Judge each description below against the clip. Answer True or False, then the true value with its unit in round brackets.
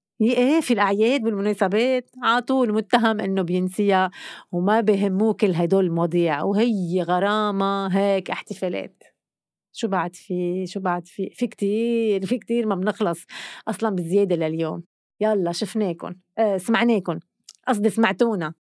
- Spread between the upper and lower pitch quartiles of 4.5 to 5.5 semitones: False (3.4 semitones)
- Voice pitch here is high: True (205 Hz)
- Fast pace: False (125 wpm)